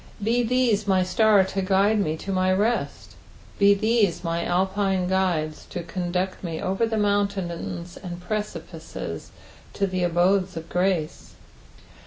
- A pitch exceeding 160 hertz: Yes, high, 190 Hz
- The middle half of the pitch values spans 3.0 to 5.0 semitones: No, narrow, 2.5 semitones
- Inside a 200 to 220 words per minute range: No, slow, 135 wpm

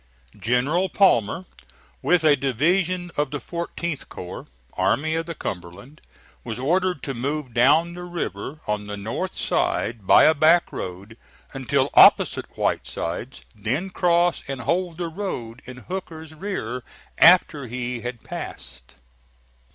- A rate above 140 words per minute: No, slow, 135 wpm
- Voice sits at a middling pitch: Yes, medium, 145 Hz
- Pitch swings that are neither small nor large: No, wide, 6.4 semitones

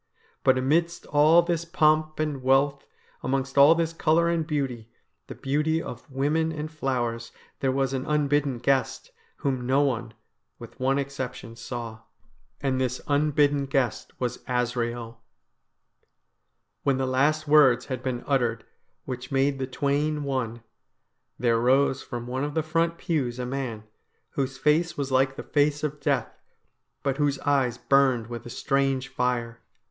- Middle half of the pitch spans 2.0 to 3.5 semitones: Yes, average, 2.9 semitones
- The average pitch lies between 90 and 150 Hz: Yes, low, 135 Hz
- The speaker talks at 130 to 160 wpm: Yes, average, 150 wpm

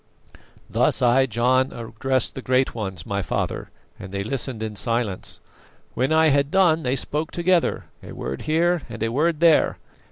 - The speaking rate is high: No, average, 165 wpm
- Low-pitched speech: Yes, low, 130 Hz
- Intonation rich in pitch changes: Yes, wide, 5.7 semitones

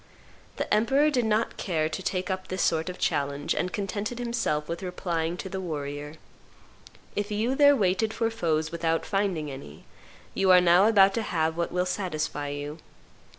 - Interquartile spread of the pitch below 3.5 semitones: No, average, 4.6 semitones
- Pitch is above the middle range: No, medium, 180 Hz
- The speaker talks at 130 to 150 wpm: No, average, 175 wpm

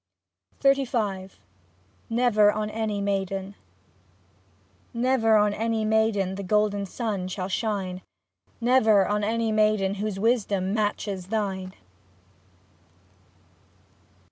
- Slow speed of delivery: Yes, slow, 90 wpm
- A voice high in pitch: Yes, high, 210 Hz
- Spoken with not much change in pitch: Yes, narrow, 2.3 semitones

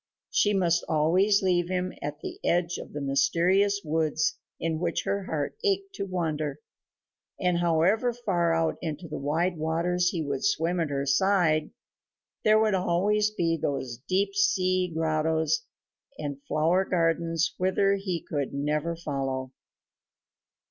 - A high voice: No, medium, 170 Hz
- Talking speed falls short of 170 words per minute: Yes, average, 140 wpm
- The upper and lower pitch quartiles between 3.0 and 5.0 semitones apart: Yes, average, 3.4 semitones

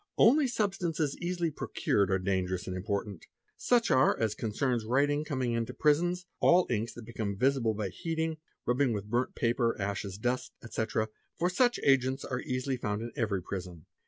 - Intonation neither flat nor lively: No, wide, 6.2 semitones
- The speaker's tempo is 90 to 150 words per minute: No, average, 165 wpm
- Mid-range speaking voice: No, low, 120 Hz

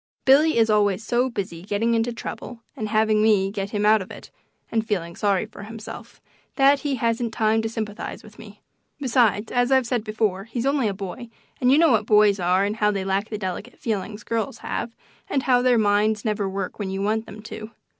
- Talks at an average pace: No, fast, 215 wpm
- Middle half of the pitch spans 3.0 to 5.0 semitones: No, narrow, 2.5 semitones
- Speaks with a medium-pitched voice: No, high, 215 Hz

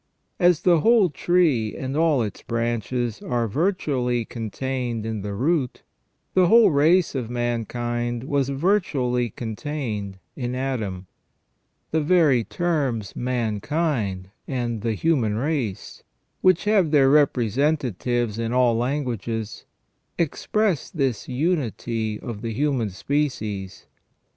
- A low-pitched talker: Yes, low, 125 Hz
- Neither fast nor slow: No, slow, 115 wpm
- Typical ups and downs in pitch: Yes, average, 4.8 semitones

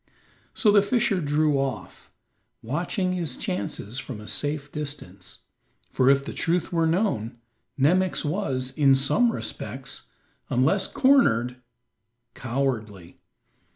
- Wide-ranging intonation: Yes, wide, 6.1 semitones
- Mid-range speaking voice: Yes, medium, 145 Hz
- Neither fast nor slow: No, slow, 115 wpm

